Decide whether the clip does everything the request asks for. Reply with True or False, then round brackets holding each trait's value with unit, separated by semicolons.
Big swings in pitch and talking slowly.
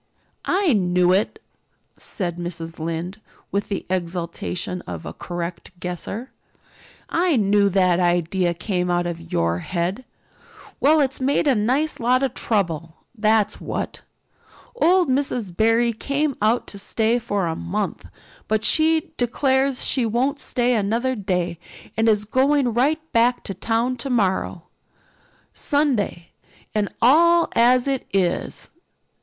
True (6.5 semitones; 130 wpm)